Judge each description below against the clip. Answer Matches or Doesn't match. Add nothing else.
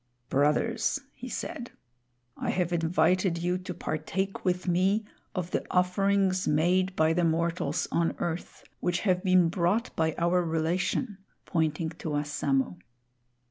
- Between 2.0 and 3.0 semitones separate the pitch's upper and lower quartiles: Matches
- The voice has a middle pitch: Matches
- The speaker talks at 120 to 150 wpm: Matches